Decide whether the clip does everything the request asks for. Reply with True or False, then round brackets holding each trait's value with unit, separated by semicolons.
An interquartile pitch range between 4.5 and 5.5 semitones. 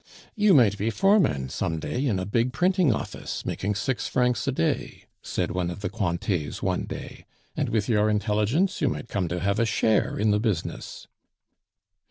True (4.9 semitones)